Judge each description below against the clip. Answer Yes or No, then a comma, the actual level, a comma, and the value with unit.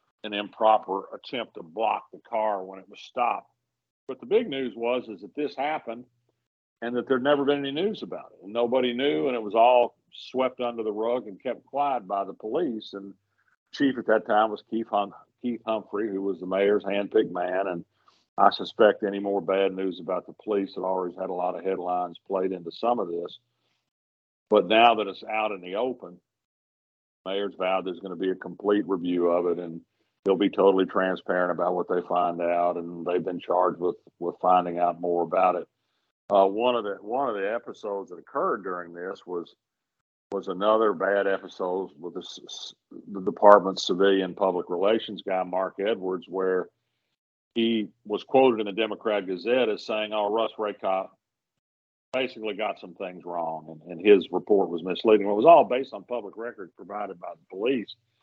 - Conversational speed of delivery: Yes, average, 195 wpm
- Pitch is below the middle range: Yes, low, 100 Hz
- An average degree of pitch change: Yes, average, 3.4 semitones